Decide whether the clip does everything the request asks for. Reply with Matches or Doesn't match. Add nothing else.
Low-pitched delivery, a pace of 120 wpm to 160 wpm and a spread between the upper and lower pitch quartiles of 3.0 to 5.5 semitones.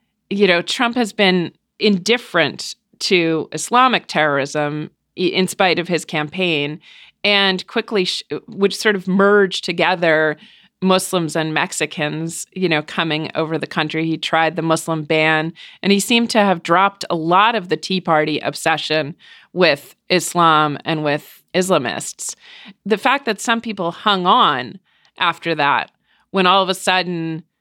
Doesn't match